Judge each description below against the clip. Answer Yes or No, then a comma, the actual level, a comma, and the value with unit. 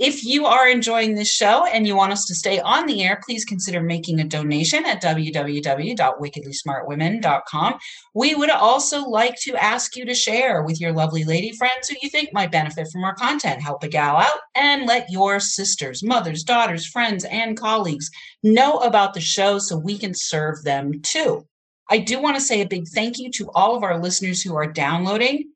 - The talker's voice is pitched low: No, high, 200 Hz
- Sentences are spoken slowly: No, average, 195 wpm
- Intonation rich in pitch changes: Yes, wide, 6.9 semitones